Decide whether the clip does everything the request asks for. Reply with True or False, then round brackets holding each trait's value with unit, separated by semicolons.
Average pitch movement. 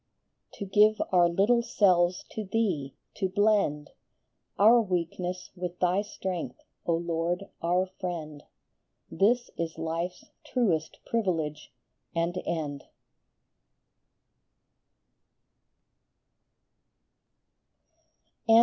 True (3.3 semitones)